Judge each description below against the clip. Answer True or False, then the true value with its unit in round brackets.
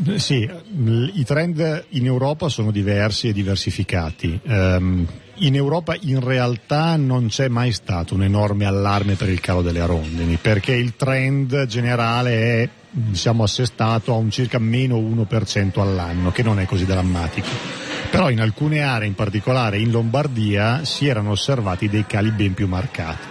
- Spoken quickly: False (150 wpm)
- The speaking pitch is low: True (115 Hz)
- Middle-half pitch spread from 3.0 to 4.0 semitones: False (4.5 semitones)